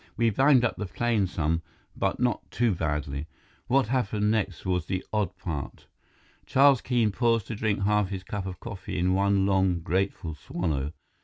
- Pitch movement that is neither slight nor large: Yes, average, 4.0 semitones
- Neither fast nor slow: Yes, average, 170 wpm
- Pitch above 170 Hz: No, low, 100 Hz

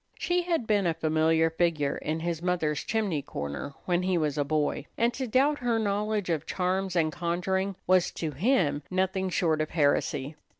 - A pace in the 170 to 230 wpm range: Yes, average, 180 wpm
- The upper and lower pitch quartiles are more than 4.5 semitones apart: No, average, 4.2 semitones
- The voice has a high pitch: No, medium, 175 Hz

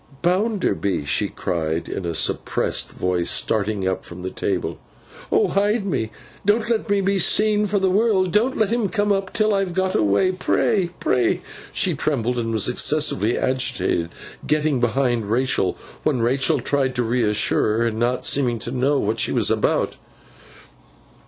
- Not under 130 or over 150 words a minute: No, average, 165 wpm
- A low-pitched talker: Yes, low, 130 Hz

